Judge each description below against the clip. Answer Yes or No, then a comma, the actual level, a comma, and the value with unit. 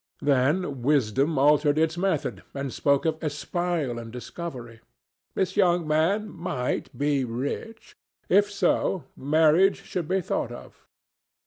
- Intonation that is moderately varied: Yes, average, 4.4 semitones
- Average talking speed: No, slow, 125 wpm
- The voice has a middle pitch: Yes, medium, 155 Hz